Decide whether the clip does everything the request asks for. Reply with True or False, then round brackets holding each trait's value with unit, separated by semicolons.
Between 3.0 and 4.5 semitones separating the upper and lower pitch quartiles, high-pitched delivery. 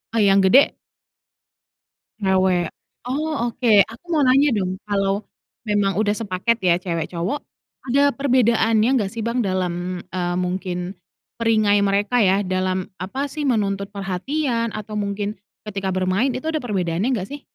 True (3.9 semitones; 200 Hz)